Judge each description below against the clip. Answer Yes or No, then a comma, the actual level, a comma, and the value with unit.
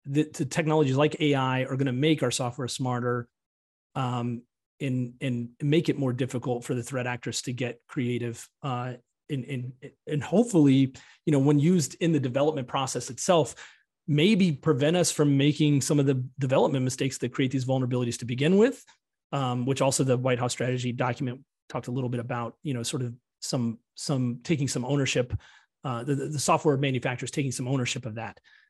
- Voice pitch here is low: Yes, low, 130 Hz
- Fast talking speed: No, average, 190 wpm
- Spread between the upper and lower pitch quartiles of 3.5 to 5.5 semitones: No, average, 3.0 semitones